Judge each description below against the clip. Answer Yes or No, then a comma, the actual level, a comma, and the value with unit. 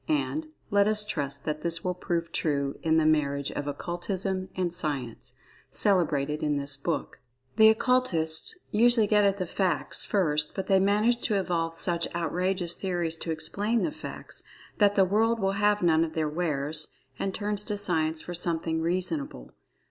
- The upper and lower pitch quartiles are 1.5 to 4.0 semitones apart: No, average, 4.4 semitones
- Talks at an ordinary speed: Yes, average, 170 wpm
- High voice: No, medium, 175 Hz